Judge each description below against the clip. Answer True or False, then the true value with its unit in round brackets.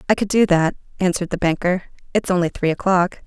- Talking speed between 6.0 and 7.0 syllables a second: True (6.3 syllables/s)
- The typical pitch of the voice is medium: True (180 Hz)